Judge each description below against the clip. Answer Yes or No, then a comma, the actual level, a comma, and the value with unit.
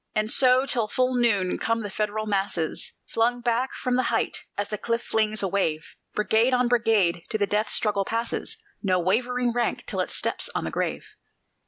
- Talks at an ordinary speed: Yes, average, 190 wpm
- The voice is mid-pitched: No, high, 220 Hz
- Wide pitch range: No, average, 3.2 semitones